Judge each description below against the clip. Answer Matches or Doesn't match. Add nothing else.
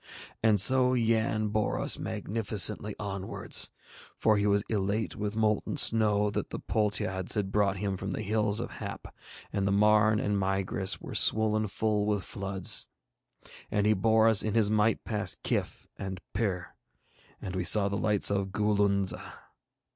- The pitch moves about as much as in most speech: Doesn't match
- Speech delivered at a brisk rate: Doesn't match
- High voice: Doesn't match